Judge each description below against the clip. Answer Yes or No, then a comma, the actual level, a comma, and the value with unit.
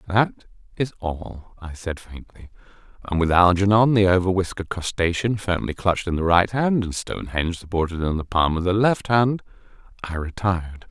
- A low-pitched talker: Yes, very low, 95 Hz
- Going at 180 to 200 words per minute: No, average, 165 wpm